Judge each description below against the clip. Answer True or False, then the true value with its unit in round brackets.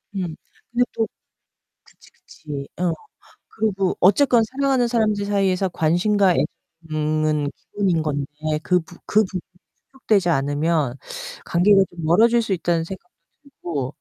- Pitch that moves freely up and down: False (5.0 semitones)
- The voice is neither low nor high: True (180 Hz)